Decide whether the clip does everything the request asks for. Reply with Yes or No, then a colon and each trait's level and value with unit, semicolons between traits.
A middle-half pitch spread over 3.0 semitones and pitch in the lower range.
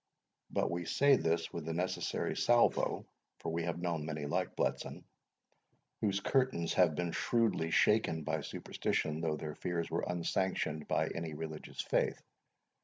No: average, 2.7 semitones; very low, 85 Hz